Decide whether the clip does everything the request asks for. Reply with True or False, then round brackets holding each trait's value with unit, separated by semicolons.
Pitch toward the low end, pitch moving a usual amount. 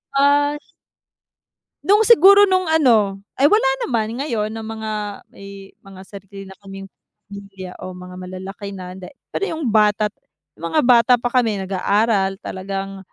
False (210 Hz; 4.5 semitones)